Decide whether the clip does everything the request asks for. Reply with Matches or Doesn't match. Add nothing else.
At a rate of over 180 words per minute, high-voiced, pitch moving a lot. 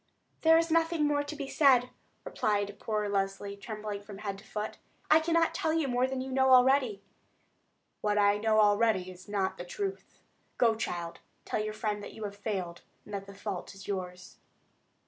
Doesn't match